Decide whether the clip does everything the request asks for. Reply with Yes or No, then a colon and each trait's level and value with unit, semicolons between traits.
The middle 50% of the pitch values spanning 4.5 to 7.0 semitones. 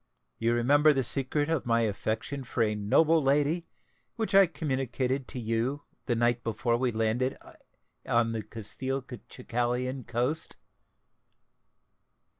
No: average, 3.3 semitones